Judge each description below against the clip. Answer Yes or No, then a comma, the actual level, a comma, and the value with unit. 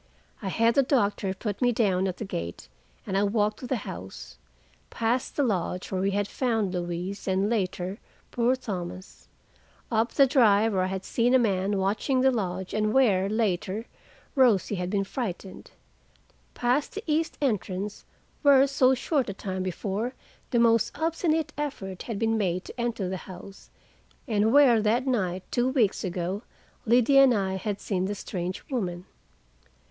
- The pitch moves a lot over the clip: No, average, 4.5 semitones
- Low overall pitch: No, high, 210 Hz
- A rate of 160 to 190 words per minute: Yes, average, 165 wpm